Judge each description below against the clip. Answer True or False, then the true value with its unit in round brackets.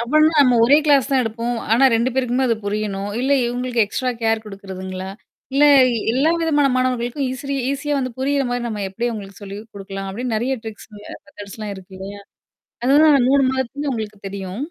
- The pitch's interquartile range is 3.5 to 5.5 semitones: True (4.8 semitones)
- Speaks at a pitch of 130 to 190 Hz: False (240 Hz)